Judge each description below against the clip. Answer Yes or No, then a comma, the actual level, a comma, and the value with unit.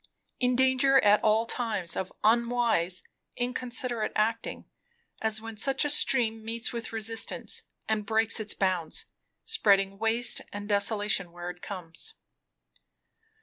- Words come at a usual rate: No, slow, 125 wpm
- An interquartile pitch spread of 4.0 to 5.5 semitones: No, average, 3.0 semitones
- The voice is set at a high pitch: Yes, high, 220 Hz